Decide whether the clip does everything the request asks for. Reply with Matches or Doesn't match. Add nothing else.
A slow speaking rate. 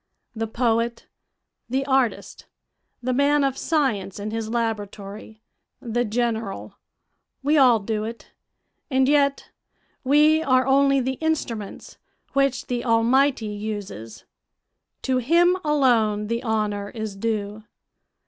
Matches